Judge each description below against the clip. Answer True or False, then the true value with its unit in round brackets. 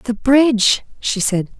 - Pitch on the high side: True (230 Hz)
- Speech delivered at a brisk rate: False (150 wpm)